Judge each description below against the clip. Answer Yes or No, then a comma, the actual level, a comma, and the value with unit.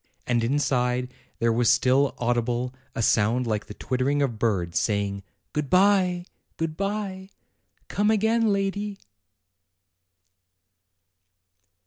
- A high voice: No, low, 130 Hz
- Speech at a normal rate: No, slow, 105 wpm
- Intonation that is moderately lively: No, wide, 8.3 semitones